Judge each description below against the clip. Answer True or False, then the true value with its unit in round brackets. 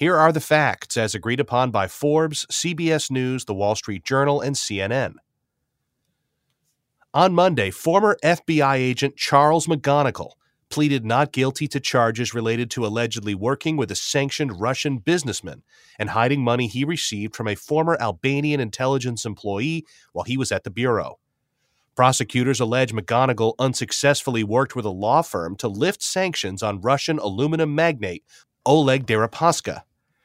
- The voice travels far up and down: False (4.5 semitones)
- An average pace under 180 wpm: True (145 wpm)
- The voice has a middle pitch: False (130 Hz)